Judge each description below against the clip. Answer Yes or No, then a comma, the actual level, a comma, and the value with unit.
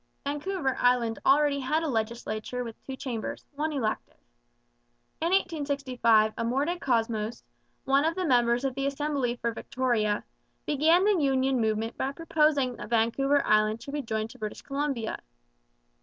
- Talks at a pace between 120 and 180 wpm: Yes, average, 145 wpm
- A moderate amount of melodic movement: Yes, average, 4.1 semitones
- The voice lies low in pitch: No, very high, 265 Hz